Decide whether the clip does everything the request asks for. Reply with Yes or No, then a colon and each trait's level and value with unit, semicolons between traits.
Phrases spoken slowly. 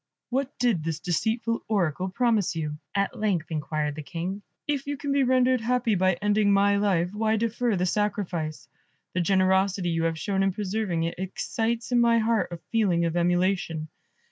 No: average, 175 wpm